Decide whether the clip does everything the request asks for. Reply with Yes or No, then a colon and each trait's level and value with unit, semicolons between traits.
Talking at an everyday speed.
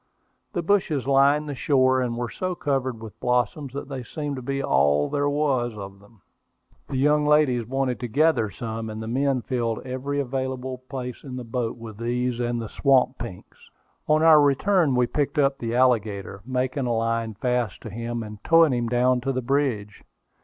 Yes: average, 190 wpm